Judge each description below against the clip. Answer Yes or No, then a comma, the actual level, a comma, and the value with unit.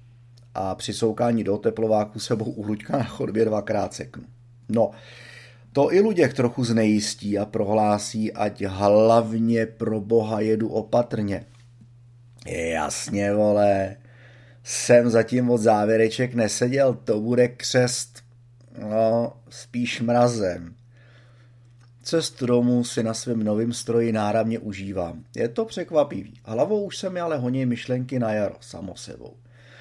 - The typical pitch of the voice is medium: No, low, 120 Hz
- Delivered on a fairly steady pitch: Yes, narrow, 1.8 semitones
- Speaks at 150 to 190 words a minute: No, average, 120 wpm